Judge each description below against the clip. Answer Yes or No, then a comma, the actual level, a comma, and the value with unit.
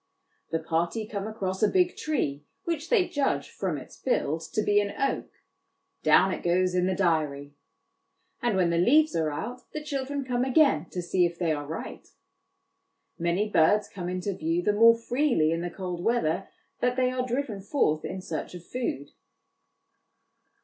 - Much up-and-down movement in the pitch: Yes, wide, 6.6 semitones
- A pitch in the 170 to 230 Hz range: Yes, high, 190 Hz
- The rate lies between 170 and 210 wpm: Yes, average, 175 wpm